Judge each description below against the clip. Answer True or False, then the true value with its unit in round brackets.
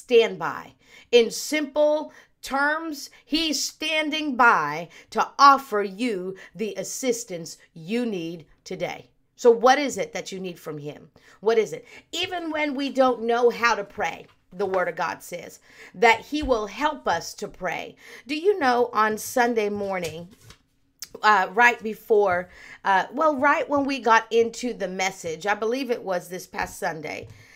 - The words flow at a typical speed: True (160 wpm)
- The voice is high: True (235 Hz)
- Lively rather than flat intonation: True (6.6 semitones)